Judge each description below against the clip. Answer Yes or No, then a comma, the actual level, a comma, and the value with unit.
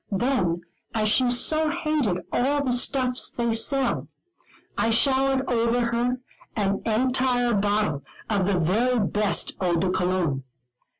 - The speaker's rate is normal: No, slow, 130 wpm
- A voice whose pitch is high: Yes, high, 235 Hz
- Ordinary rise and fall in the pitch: Yes, average, 4.8 semitones